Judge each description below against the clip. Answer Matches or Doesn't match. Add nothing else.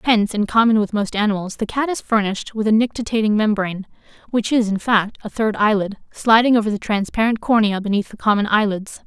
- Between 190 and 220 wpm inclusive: Matches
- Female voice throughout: Matches